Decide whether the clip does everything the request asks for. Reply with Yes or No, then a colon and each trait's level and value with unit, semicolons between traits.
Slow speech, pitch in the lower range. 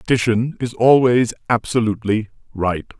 Yes: slow, 100 wpm; low, 115 Hz